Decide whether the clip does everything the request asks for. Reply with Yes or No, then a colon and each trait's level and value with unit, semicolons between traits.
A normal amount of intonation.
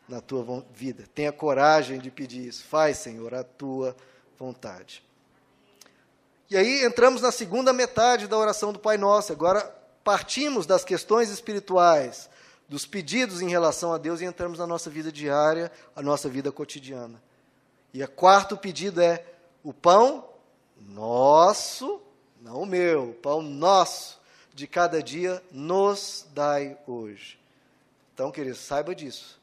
No: wide, 6.3 semitones